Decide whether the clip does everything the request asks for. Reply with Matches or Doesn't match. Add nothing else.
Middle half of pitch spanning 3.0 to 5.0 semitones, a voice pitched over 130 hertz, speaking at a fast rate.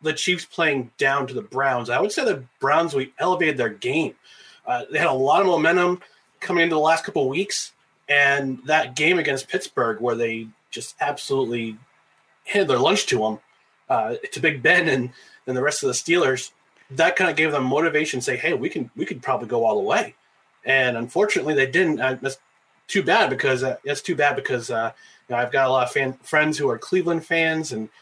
Matches